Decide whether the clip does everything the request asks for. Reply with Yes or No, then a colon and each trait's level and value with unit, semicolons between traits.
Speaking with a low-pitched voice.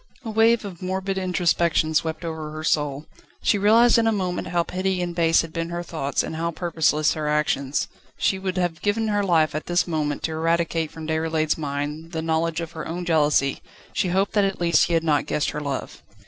No: medium, 165 Hz